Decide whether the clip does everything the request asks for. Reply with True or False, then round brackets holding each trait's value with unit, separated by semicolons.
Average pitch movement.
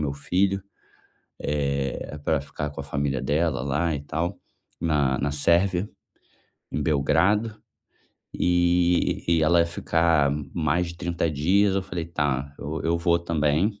True (3.4 semitones)